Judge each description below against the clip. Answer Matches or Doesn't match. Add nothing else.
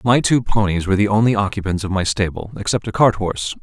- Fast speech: Matches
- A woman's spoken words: Doesn't match